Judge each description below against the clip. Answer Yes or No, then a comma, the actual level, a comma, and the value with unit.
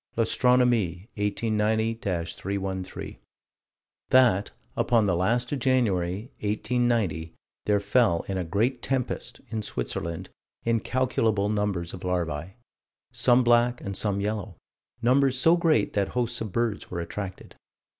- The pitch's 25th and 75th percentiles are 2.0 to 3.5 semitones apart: No, average, 4.3 semitones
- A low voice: Yes, low, 105 Hz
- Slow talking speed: Yes, slow, 120 wpm